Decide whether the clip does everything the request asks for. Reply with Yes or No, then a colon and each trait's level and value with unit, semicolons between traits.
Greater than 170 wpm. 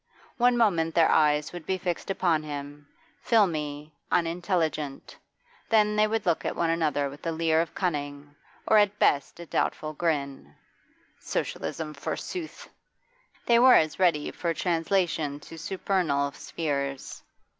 No: slow, 135 wpm